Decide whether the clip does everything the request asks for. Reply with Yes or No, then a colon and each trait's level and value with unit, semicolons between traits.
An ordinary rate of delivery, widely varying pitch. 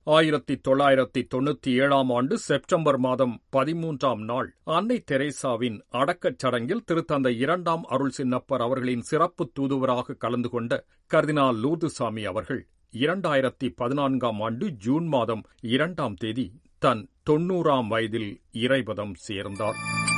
No: average, 110 wpm; average, 3.5 semitones